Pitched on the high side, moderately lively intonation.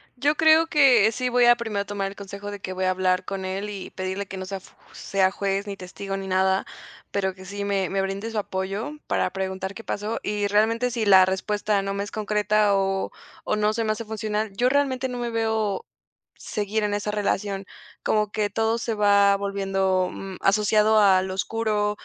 No: high, 205 Hz; narrow, 2.1 semitones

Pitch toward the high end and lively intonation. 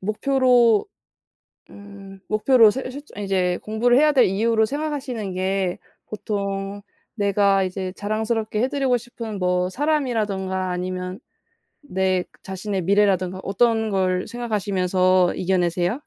No: high, 200 Hz; average, 3.8 semitones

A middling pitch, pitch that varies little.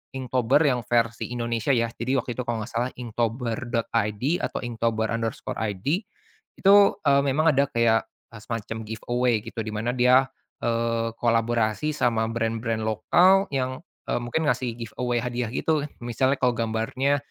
No: low, 120 Hz; narrow, 2.2 semitones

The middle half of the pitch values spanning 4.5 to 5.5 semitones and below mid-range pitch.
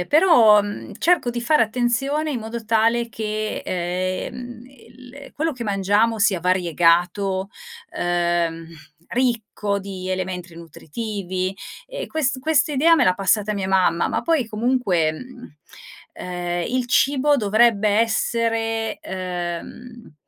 No: average, 4.9 semitones; high, 215 Hz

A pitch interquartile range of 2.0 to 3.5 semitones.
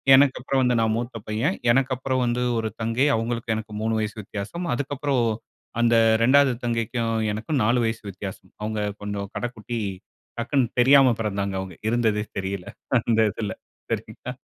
Yes: average, 2.8 semitones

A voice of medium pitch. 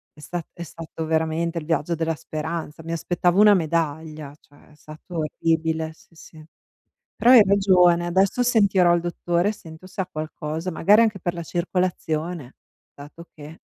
Yes: medium, 165 Hz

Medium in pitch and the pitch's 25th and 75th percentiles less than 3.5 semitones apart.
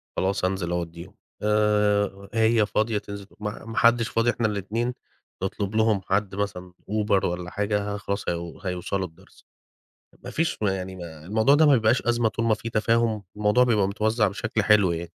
No: low, 105 Hz; narrow, 2.6 semitones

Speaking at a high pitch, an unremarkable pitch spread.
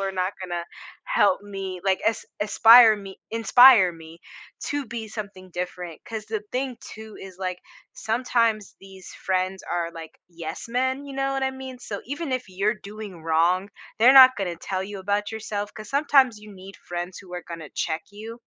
Yes: high, 205 Hz; average, 4.3 semitones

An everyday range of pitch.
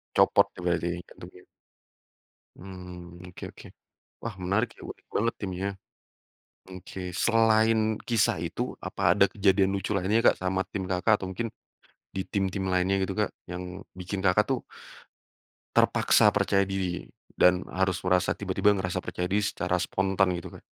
No: narrow, 1.8 semitones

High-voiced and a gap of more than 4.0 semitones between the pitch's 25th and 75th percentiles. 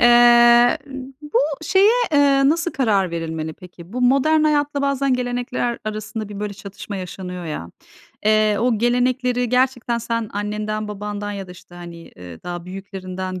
Yes: high, 215 Hz; average, 4.9 semitones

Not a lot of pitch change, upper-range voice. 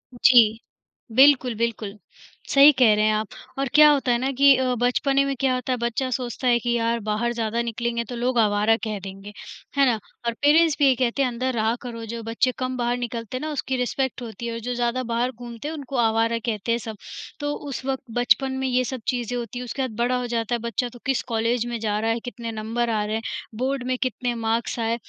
Yes: narrow, 2.1 semitones; high, 240 Hz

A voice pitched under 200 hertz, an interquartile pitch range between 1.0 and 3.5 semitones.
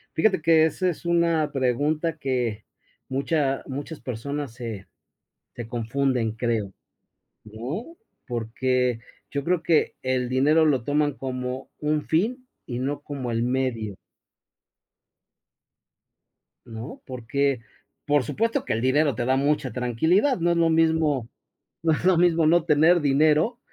No: medium, 140 Hz; average, 4.5 semitones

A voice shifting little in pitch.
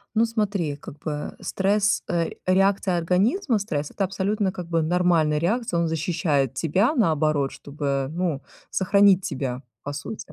No: average, 4.8 semitones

